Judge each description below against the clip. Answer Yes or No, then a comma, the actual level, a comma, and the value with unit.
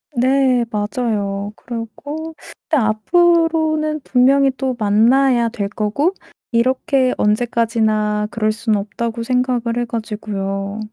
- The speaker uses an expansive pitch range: No, average, 4.0 semitones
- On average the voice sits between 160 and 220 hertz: No, high, 235 Hz